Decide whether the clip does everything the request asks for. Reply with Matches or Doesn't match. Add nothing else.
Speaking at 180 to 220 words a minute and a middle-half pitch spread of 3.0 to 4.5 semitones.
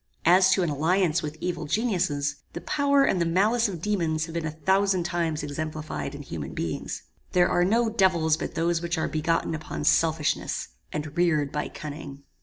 Matches